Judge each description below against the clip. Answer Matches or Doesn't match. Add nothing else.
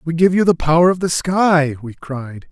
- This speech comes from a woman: Doesn't match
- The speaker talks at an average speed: Doesn't match